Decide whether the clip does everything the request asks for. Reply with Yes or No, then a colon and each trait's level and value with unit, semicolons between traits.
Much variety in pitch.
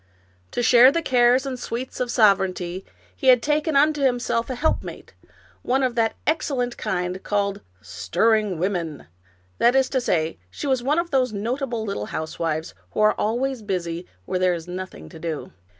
Yes: wide, 6.4 semitones